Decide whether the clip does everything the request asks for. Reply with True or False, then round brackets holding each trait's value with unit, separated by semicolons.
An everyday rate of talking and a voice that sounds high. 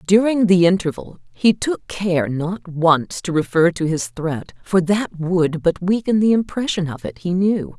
False (185 wpm; 180 Hz)